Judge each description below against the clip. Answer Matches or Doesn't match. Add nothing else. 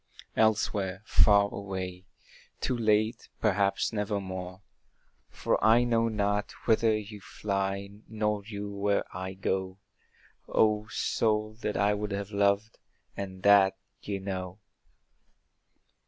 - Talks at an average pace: Doesn't match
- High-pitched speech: Doesn't match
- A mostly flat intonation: Matches